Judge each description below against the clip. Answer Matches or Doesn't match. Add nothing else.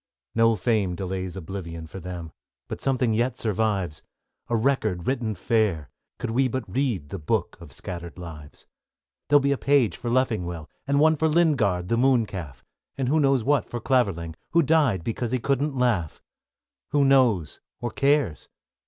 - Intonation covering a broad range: Matches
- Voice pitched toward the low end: Matches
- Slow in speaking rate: Doesn't match